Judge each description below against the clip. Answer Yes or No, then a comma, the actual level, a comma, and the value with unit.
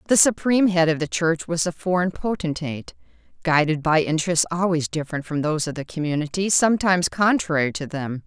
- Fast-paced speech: No, average, 175 wpm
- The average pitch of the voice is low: No, medium, 165 Hz